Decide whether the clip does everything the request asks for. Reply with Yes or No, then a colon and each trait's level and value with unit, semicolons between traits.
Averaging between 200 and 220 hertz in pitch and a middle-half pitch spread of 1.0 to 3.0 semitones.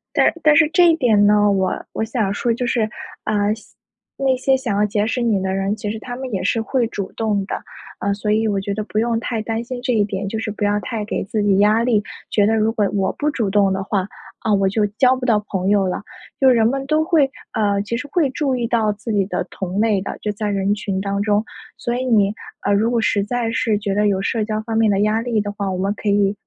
Yes: high, 215 Hz; narrow, 2.6 semitones